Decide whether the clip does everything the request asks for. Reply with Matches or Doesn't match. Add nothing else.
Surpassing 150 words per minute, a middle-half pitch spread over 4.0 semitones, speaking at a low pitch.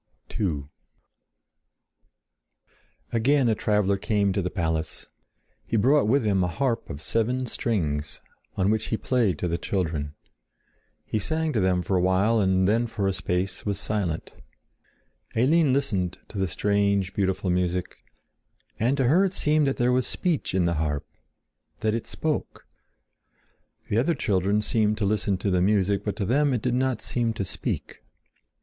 Matches